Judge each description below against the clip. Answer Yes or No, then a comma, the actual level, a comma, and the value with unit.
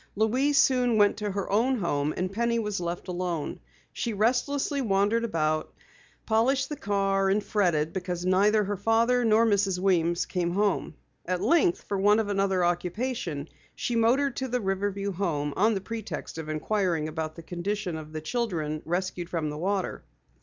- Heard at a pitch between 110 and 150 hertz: No, high, 195 Hz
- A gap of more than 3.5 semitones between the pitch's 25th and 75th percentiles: Yes, average, 4.4 semitones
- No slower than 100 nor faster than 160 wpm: No, average, 170 wpm